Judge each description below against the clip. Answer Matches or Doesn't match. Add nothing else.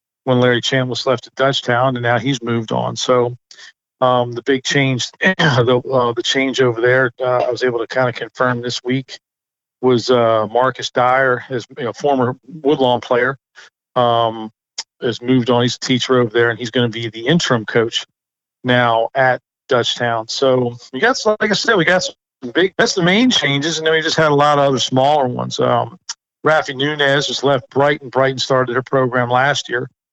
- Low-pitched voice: Matches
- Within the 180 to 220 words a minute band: Matches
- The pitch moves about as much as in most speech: Doesn't match